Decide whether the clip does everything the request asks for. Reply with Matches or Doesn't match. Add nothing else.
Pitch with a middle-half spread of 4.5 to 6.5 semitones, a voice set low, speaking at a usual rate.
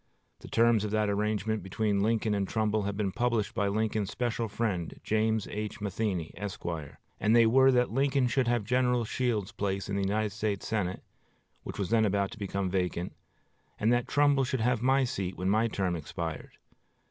Doesn't match